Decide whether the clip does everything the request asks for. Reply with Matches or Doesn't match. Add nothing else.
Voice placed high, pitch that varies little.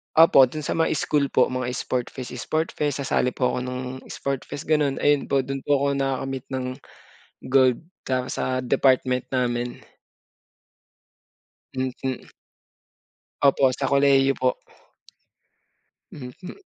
Doesn't match